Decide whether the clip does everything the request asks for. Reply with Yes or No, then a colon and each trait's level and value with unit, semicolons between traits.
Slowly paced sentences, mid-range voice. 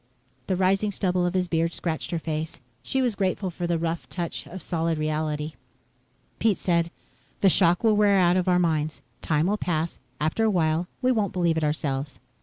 No: average, 195 wpm; medium, 175 Hz